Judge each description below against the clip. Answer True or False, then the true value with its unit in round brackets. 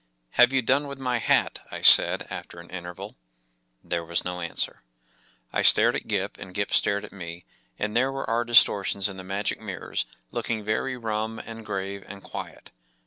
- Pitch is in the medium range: False (105 Hz)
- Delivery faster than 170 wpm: True (180 wpm)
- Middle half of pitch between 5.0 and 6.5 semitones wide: False (4.1 semitones)